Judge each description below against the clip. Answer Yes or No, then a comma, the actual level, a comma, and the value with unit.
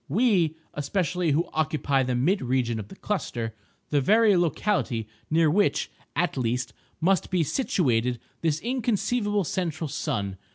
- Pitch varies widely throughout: Yes, wide, 7.1 semitones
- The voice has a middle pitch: Yes, medium, 160 Hz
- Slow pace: Yes, slow, 130 wpm